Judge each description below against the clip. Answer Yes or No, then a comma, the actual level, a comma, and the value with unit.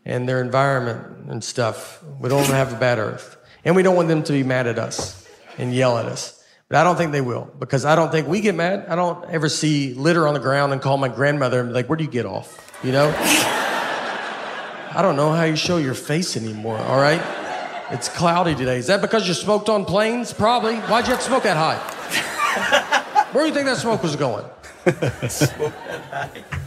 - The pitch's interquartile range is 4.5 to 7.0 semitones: Yes, average, 5.2 semitones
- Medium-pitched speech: Yes, medium, 155 Hz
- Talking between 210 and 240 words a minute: Yes, average, 220 wpm